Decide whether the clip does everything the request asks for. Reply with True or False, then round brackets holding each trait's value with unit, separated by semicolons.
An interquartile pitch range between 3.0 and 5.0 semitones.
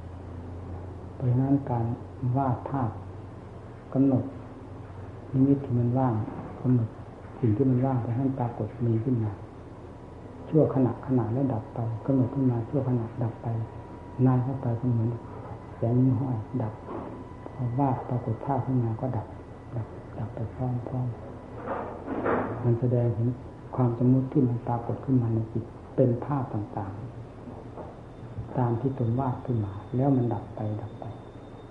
False (2.6 semitones)